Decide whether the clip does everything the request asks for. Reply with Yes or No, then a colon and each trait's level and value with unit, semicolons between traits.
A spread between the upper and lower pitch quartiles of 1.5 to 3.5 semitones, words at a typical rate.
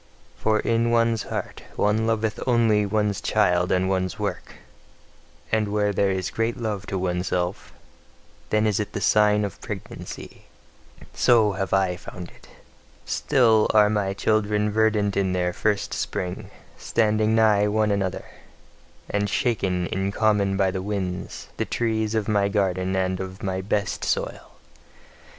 Yes: narrow, 2.4 semitones; average, 145 wpm